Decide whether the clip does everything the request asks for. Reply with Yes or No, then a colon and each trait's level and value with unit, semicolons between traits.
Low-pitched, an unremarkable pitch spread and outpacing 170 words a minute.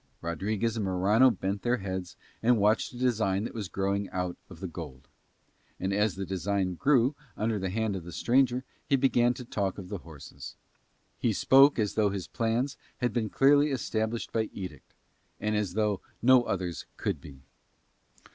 Yes: low, 105 Hz; average, 4.2 semitones; average, 180 wpm